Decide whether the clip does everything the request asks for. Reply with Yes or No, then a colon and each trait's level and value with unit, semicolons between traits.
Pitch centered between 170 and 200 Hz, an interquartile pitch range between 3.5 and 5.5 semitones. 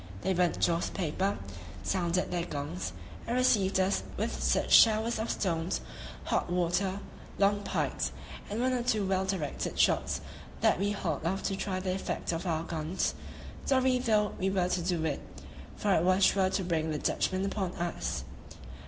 No: high, 190 Hz; average, 2.9 semitones